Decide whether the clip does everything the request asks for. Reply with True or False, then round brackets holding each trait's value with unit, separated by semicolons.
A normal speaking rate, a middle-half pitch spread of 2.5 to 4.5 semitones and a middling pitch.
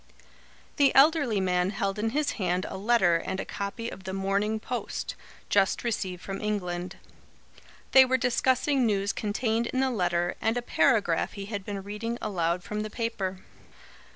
False (165 wpm; 3.7 semitones; 205 Hz)